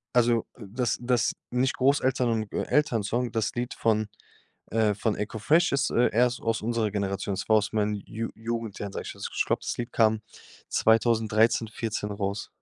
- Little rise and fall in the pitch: Yes, narrow, 2.3 semitones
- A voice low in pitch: Yes, low, 115 Hz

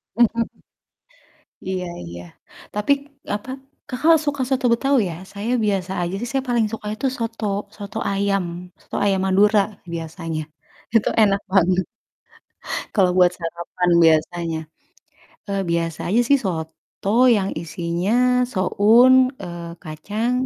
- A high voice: Yes, high, 195 Hz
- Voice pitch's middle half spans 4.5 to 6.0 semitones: Yes, average, 4.8 semitones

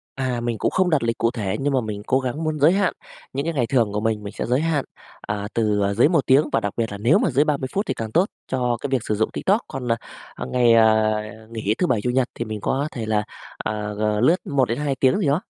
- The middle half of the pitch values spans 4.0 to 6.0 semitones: Yes, average, 4.5 semitones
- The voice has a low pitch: Yes, low, 125 Hz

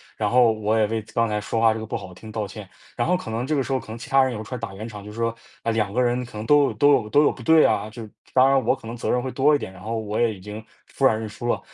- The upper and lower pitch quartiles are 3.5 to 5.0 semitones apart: No, average, 3.0 semitones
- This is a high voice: No, low, 115 Hz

